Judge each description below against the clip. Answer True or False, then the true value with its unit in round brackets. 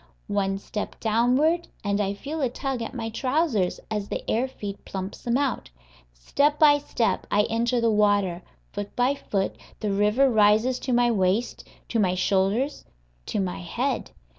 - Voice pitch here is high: True (225 Hz)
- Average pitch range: True (4.1 semitones)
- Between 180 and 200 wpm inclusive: False (165 wpm)